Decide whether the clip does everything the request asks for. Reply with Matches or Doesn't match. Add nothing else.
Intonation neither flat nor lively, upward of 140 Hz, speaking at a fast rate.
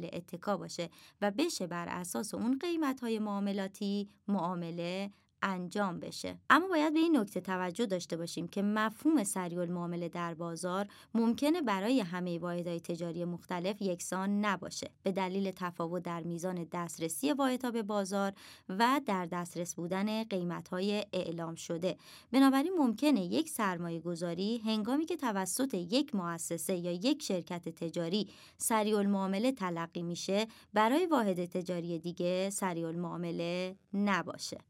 Doesn't match